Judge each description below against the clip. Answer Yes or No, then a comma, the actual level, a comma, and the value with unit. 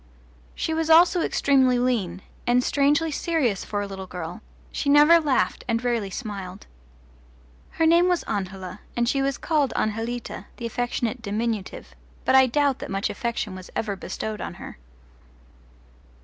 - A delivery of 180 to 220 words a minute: No, average, 150 wpm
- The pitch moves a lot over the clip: Yes, wide, 5.8 semitones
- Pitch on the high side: Yes, high, 240 Hz